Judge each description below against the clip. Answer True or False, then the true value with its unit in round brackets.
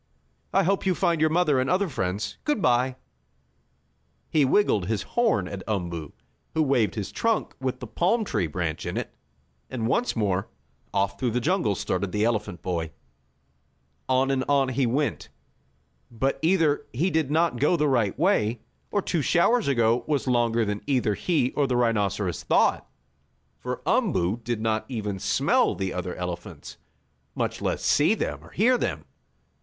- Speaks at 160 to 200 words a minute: True (165 wpm)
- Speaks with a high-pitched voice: False (125 Hz)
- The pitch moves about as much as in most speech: False (7.1 semitones)